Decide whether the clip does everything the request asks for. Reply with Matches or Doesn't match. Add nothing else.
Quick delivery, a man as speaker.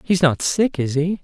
Matches